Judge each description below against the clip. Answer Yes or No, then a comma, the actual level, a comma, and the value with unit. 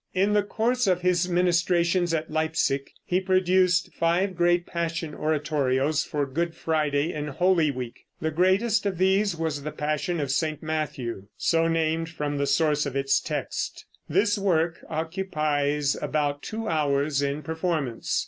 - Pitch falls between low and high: Yes, medium, 160 Hz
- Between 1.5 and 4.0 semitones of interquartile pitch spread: Yes, average, 3.4 semitones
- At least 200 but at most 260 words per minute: No, average, 150 wpm